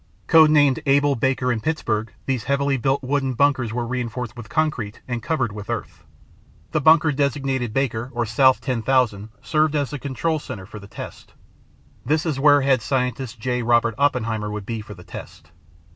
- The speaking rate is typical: Yes, average, 175 wpm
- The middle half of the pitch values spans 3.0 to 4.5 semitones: Yes, average, 3.7 semitones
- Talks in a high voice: No, low, 130 Hz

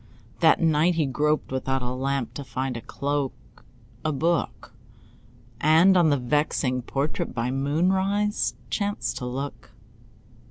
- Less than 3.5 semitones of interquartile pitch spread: No, average, 3.8 semitones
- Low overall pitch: No, medium, 145 Hz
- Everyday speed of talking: No, slow, 130 wpm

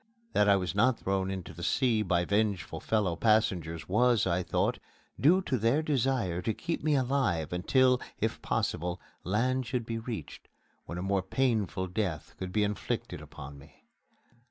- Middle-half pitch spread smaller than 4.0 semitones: No, wide, 5.6 semitones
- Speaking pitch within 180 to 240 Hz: No, low, 105 Hz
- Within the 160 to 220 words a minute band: Yes, average, 165 wpm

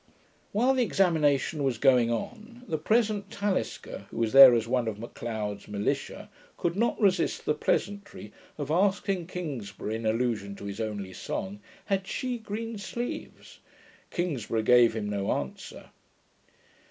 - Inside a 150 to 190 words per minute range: No, average, 140 wpm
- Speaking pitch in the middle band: Yes, medium, 145 Hz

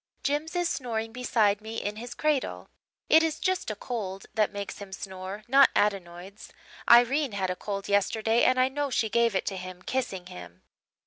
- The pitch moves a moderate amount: Yes, average, 4.7 semitones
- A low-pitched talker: No, high, 220 Hz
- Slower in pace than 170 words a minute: No, average, 185 wpm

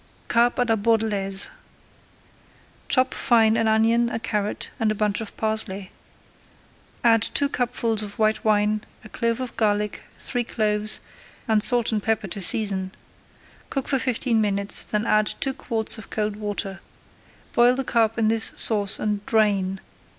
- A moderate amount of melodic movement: No, narrow, 1.9 semitones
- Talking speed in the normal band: Yes, average, 155 wpm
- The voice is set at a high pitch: Yes, high, 220 Hz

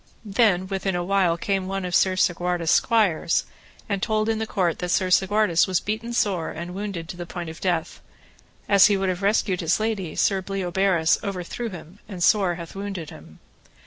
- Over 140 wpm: Yes, average, 190 wpm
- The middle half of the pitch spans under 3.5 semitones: Yes, narrow, 2.4 semitones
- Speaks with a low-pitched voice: No, high, 190 Hz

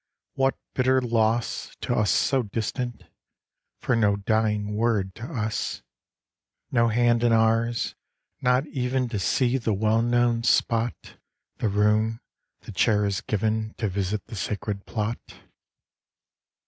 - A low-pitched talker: Yes, low, 115 Hz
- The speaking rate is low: Yes, slow, 130 wpm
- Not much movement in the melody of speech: Yes, narrow, 2.2 semitones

